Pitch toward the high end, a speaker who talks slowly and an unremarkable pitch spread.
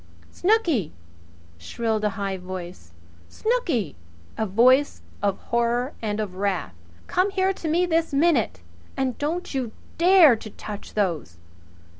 No: high, 235 Hz; slow, 130 wpm; wide, 8.6 semitones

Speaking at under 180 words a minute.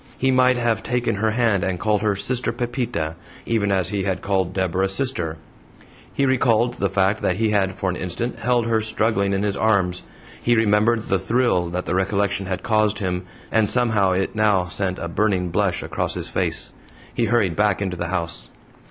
No: average, 195 wpm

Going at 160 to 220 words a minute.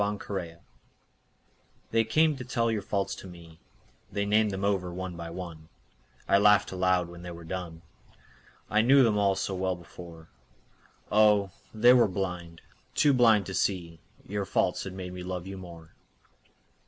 Yes: average, 165 wpm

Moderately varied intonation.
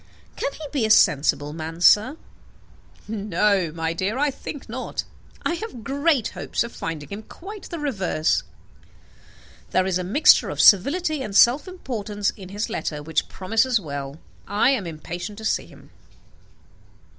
No: wide, 7.6 semitones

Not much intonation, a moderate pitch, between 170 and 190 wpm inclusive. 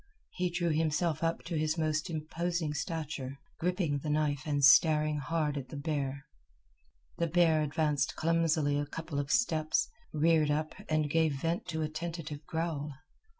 No: narrow, 1.9 semitones; medium, 155 Hz; average, 155 wpm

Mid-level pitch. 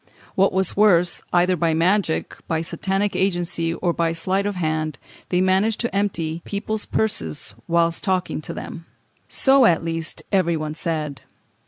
Yes: medium, 175 Hz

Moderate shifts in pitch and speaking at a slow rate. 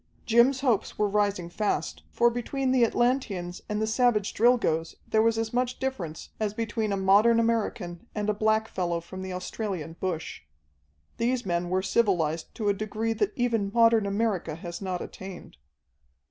No: average, 3.7 semitones; average, 160 wpm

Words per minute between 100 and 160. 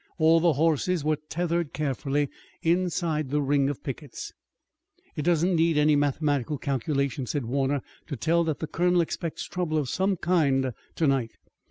Yes: average, 155 wpm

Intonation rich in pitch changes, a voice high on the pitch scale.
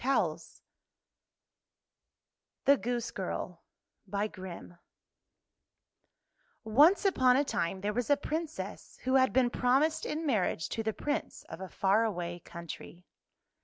Yes: wide, 6.8 semitones; high, 240 Hz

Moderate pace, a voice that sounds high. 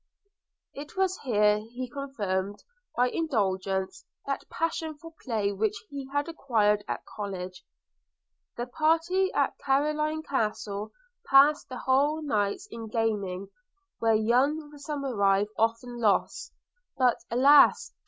No: slow, 115 wpm; high, 245 Hz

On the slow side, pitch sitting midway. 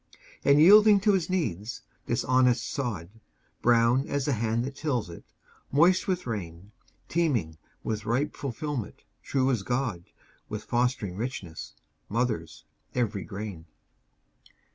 No: slow, 125 wpm; low, 120 Hz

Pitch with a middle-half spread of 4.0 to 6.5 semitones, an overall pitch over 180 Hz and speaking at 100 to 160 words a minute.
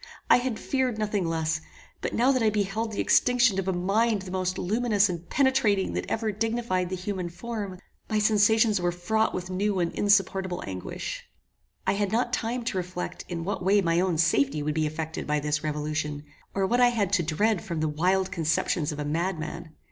No: average, 4.5 semitones; high, 190 Hz; average, 200 wpm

